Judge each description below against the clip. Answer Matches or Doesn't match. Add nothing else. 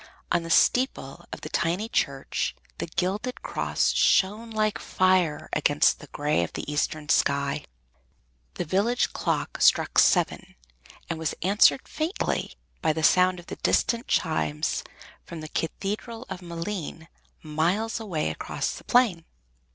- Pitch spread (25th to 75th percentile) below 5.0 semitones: Doesn't match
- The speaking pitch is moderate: Matches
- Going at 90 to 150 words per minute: Matches